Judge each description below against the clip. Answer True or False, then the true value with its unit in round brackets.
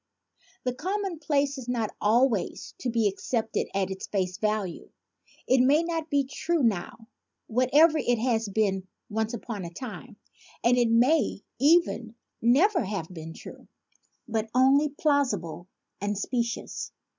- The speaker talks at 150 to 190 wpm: False (140 wpm)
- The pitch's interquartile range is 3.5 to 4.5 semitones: False (5.1 semitones)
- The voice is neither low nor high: False (235 Hz)